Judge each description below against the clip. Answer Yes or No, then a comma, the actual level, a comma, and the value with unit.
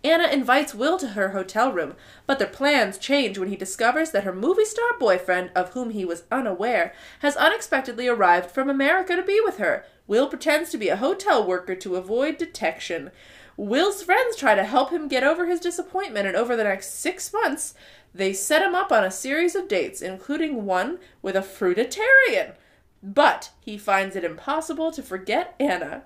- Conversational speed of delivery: Yes, average, 185 wpm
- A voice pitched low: No, very high, 275 Hz